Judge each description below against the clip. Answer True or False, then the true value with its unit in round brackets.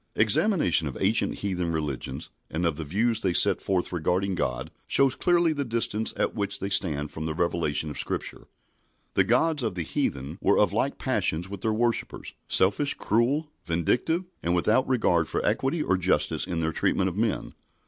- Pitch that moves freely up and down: True (6.1 semitones)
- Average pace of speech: True (180 wpm)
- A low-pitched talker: True (95 Hz)